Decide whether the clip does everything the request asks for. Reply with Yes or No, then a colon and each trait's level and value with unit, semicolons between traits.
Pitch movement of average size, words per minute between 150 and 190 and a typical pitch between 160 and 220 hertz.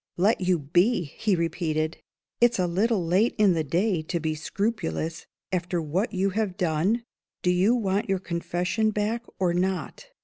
Yes: average, 3.7 semitones; average, 165 wpm; medium, 185 Hz